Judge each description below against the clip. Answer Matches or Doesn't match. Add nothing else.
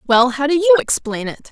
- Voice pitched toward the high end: Matches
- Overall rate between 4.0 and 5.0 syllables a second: Doesn't match